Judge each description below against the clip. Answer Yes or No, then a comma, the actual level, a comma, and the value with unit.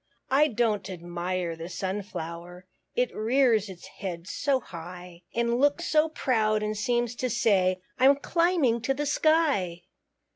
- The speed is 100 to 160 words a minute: Yes, average, 140 wpm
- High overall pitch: Yes, high, 215 Hz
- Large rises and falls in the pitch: Yes, wide, 6.6 semitones